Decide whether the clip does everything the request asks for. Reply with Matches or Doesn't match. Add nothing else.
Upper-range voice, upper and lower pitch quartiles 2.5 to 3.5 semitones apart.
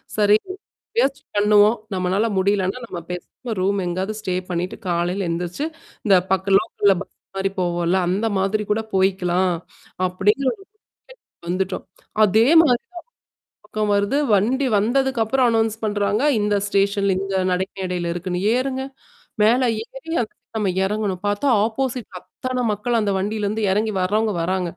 Matches